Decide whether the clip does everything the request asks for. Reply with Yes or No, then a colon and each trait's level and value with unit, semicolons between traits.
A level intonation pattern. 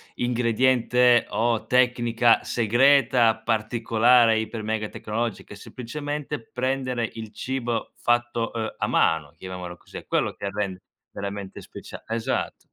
Yes: narrow, 2.2 semitones